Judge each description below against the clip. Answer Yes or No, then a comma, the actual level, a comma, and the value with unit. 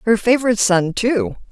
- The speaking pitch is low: No, high, 225 Hz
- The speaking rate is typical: Yes, average, 160 wpm